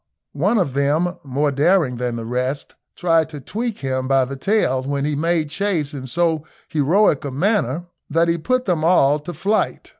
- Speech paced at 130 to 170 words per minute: No, average, 185 wpm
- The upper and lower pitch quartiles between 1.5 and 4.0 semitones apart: No, average, 4.4 semitones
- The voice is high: No, medium, 150 Hz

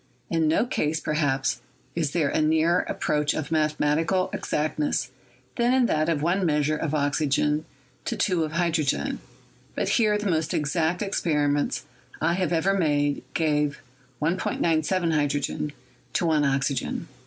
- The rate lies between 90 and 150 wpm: Yes, average, 145 wpm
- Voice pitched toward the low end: No, medium, 155 Hz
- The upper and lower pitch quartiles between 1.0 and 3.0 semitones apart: Yes, narrow, 2.5 semitones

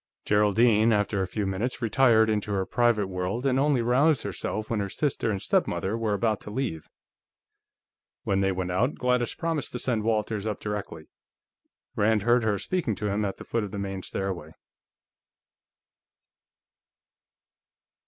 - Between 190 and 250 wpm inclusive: No, average, 155 wpm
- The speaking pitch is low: Yes, low, 105 Hz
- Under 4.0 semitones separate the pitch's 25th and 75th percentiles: Yes, average, 3.3 semitones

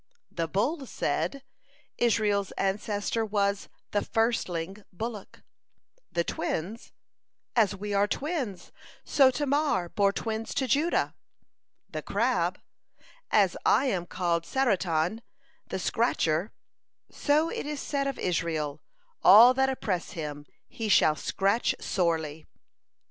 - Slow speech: Yes, slow, 115 wpm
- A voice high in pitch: Yes, high, 205 Hz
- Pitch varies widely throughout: Yes, wide, 5.8 semitones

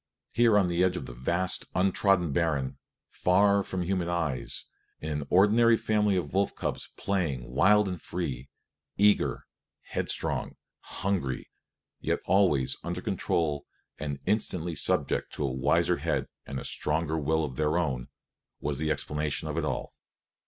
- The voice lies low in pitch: Yes, very low, 85 Hz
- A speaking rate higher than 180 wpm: No, average, 150 wpm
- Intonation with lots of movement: No, average, 5.0 semitones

